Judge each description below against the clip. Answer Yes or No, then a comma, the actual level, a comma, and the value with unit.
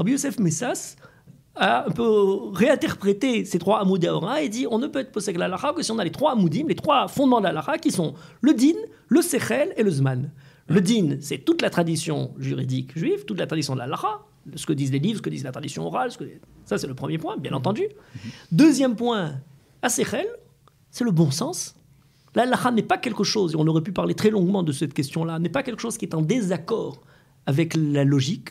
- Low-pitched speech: No, high, 190 Hz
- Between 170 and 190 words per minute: No, fast, 220 wpm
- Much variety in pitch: Yes, wide, 7.5 semitones